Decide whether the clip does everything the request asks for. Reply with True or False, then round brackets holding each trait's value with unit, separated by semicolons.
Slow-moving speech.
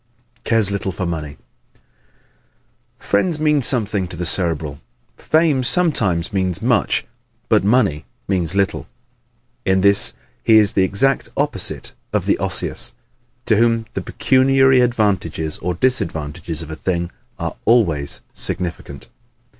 True (130 wpm)